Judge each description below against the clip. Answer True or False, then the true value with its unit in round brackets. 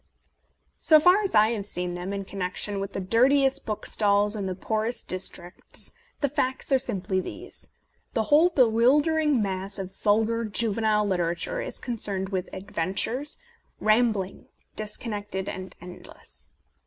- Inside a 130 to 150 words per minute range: True (140 wpm)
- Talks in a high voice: True (210 Hz)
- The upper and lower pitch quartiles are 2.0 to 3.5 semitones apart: False (4.3 semitones)